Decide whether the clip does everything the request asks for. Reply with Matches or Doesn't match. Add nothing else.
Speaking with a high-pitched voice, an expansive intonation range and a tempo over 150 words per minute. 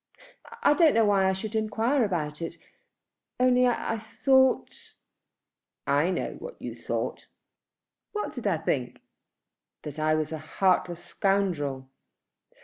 Doesn't match